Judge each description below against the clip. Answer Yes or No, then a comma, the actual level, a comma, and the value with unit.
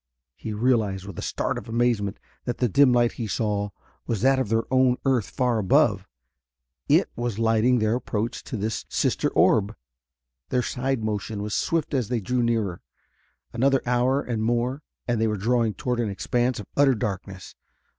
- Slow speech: No, average, 175 wpm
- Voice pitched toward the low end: Yes, low, 115 Hz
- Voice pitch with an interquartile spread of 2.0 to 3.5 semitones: Yes, average, 2.7 semitones